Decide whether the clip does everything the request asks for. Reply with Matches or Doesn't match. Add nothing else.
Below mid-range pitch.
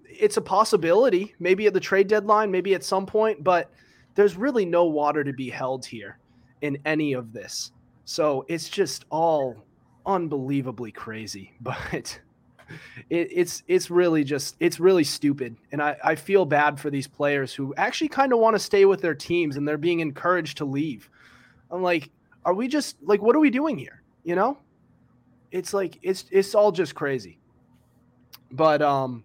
Doesn't match